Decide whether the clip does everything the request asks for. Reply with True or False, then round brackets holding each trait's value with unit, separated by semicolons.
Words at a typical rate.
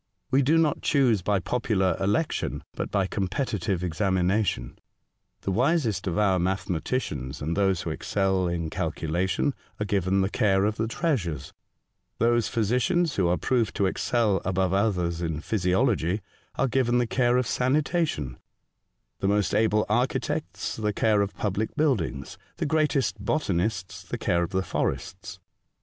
True (150 wpm)